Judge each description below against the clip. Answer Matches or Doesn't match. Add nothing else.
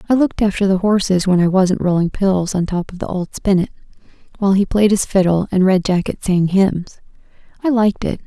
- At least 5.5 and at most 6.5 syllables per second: Matches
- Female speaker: Matches